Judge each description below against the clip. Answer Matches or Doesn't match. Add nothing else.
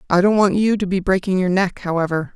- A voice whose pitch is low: Doesn't match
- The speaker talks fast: Matches